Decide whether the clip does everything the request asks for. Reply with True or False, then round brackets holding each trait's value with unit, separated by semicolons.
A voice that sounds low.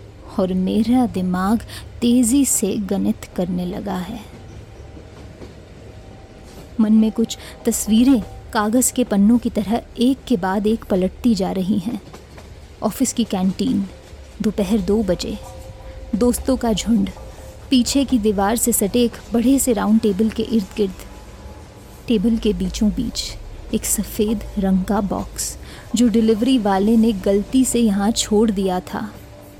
False (215 Hz)